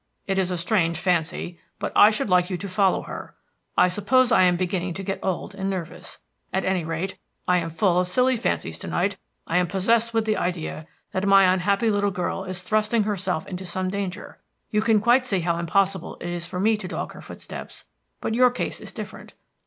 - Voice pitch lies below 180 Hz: No, high, 190 Hz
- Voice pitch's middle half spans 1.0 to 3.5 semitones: Yes, average, 2.7 semitones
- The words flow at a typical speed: No, fast, 210 wpm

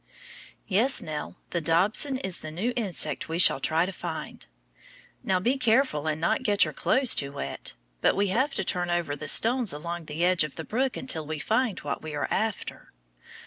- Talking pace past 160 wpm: Yes, average, 195 wpm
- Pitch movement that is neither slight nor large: No, wide, 6.3 semitones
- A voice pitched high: No, medium, 180 Hz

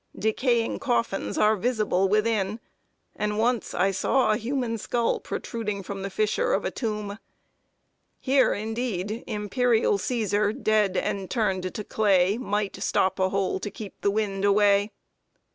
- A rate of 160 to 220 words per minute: No, average, 145 wpm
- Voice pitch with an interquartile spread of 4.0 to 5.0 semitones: No, narrow, 2.6 semitones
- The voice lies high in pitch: Yes, high, 210 Hz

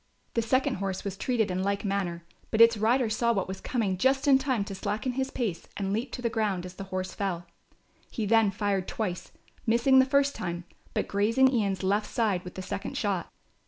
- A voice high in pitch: Yes, high, 205 Hz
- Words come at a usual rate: No, fast, 210 wpm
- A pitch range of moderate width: Yes, average, 3.7 semitones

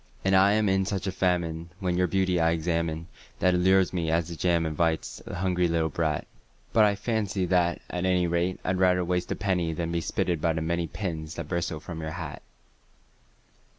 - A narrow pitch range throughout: Yes, narrow, 2.1 semitones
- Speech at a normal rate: No, fast, 210 wpm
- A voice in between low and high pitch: No, very low, 90 Hz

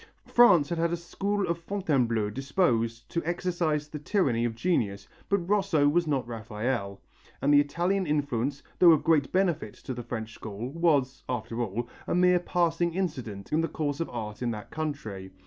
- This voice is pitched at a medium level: Yes, medium, 145 Hz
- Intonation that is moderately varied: No, wide, 6.7 semitones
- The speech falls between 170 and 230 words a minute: Yes, average, 180 wpm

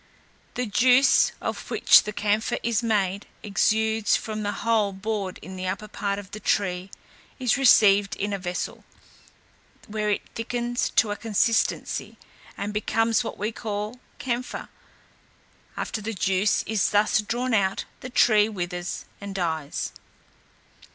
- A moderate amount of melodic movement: No, narrow, 2.3 semitones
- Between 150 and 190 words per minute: No, average, 140 wpm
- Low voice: No, high, 210 Hz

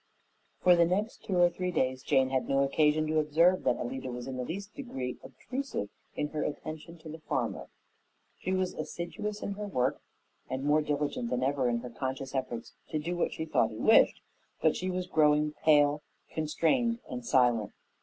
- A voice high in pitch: No, medium, 150 Hz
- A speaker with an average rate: Yes, average, 190 wpm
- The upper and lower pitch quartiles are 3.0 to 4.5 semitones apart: No, average, 5.1 semitones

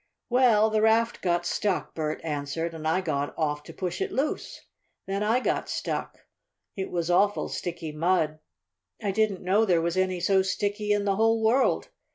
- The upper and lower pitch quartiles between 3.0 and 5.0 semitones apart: Yes, average, 4.2 semitones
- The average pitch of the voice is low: No, medium, 185 Hz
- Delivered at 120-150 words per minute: No, average, 180 wpm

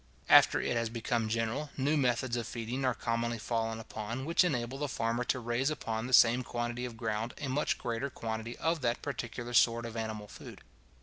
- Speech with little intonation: Yes, narrow, 2.1 semitones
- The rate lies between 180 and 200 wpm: Yes, average, 195 wpm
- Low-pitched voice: Yes, low, 120 Hz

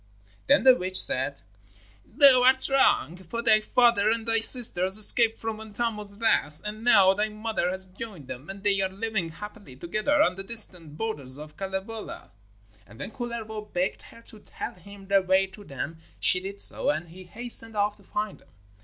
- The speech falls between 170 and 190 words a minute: Yes, average, 185 wpm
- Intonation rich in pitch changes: No, average, 3.5 semitones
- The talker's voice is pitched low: No, high, 205 Hz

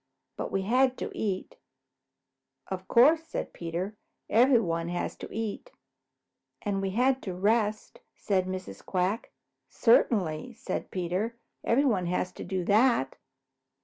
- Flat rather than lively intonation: No, average, 4.2 semitones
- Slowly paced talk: Yes, slow, 125 wpm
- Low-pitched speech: No, high, 200 Hz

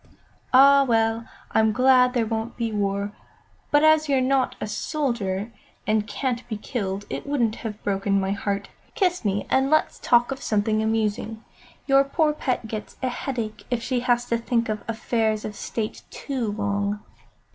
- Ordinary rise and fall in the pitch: Yes, average, 3.5 semitones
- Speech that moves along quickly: No, average, 170 wpm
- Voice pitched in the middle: No, high, 225 Hz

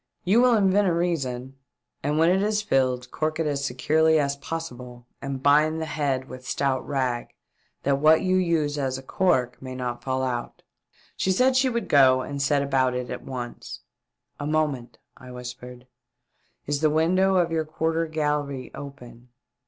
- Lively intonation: No, average, 4.0 semitones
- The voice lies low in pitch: No, medium, 145 Hz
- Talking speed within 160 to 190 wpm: Yes, average, 175 wpm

